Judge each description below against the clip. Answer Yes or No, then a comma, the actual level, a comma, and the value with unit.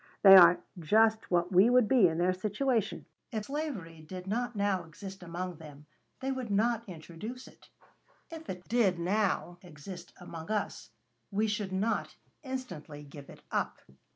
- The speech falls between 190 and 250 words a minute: No, average, 155 wpm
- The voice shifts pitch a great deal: No, average, 4.5 semitones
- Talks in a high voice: Yes, high, 195 Hz